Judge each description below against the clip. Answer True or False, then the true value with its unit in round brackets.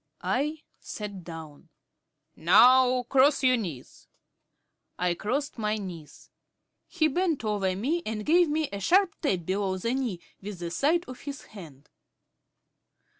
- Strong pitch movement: True (7.4 semitones)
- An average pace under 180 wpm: True (135 wpm)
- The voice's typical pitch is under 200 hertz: False (220 Hz)